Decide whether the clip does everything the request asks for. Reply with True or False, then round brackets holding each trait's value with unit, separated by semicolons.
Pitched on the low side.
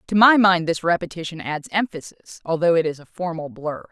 False (170 Hz)